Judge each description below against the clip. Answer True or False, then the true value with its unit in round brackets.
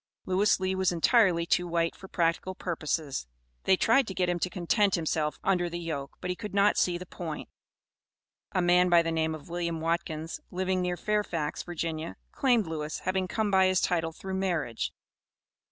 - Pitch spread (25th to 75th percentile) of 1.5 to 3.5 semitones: True (2.4 semitones)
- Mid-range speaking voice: True (175 Hz)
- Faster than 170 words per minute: True (185 wpm)